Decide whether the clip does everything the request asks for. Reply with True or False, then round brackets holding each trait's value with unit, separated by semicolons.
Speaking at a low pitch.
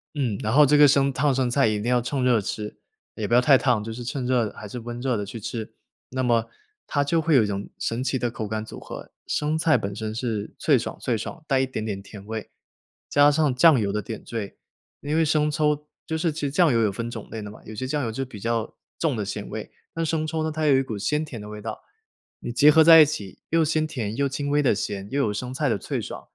True (125 Hz)